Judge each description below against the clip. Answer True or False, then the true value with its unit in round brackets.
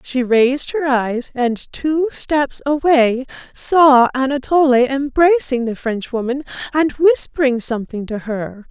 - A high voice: True (265 Hz)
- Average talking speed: False (125 wpm)